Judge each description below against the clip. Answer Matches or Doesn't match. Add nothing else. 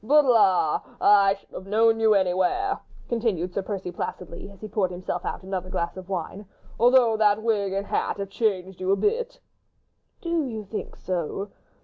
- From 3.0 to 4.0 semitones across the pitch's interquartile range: Matches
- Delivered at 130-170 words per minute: Doesn't match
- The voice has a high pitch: Matches